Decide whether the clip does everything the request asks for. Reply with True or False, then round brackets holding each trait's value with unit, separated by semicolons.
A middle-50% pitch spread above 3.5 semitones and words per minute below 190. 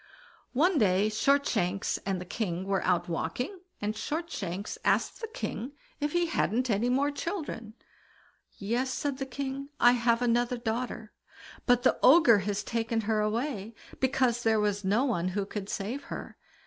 True (4.5 semitones; 160 wpm)